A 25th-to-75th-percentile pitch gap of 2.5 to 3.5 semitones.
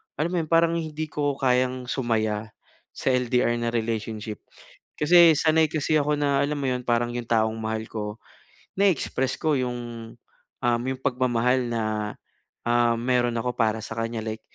No: average, 3.9 semitones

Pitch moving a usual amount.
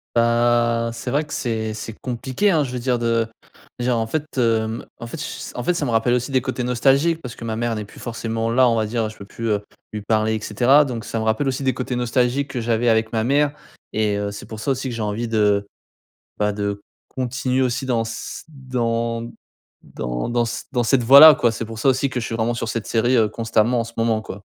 No: narrow, 2.3 semitones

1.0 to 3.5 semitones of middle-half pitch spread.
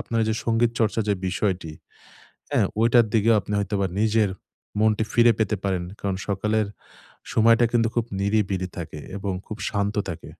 Yes: narrow, 2.5 semitones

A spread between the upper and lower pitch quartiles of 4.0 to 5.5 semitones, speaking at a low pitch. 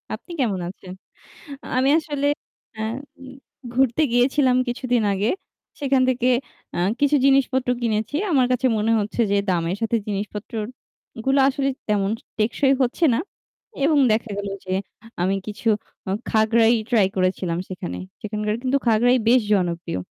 No: average, 4.3 semitones; high, 230 Hz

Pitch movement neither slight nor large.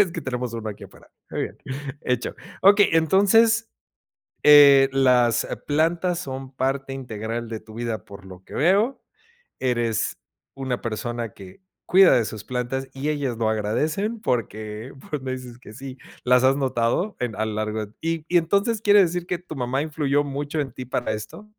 No: wide, 5.7 semitones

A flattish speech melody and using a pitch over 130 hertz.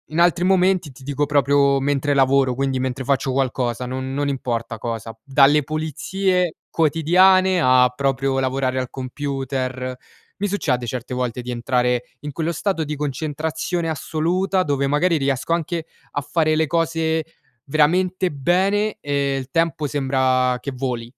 No: average, 3.9 semitones; medium, 140 Hz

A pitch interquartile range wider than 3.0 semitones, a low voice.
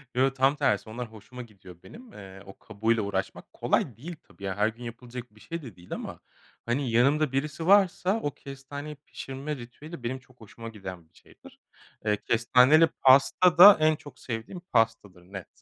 Yes: average, 5.2 semitones; low, 125 Hz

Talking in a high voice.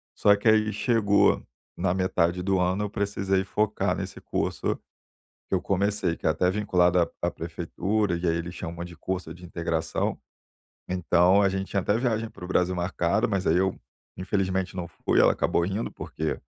No: very low, 95 Hz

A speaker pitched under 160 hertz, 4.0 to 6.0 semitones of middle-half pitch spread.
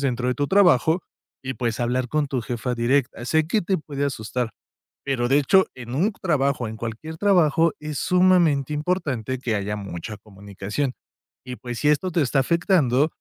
Yes: low, 135 Hz; average, 4.6 semitones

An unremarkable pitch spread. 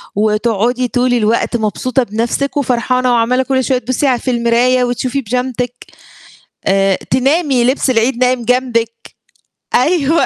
No: narrow, 1.8 semitones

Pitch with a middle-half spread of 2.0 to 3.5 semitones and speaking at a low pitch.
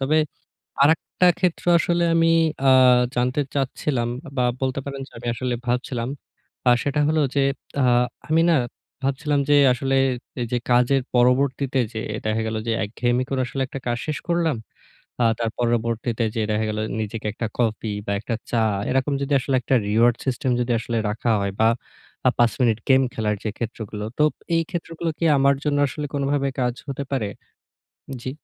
Yes: average, 3.2 semitones; low, 125 Hz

